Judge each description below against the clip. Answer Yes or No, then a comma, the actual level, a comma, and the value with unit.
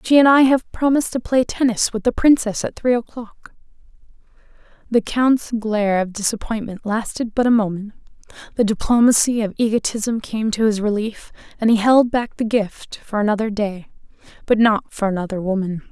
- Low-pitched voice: No, high, 220 Hz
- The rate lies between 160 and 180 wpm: Yes, average, 170 wpm